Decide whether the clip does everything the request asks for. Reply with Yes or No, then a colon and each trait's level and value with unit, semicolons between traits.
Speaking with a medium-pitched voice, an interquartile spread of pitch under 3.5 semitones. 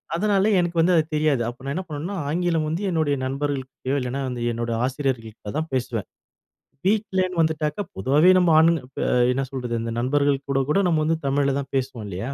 No: medium, 145 Hz; average, 4.1 semitones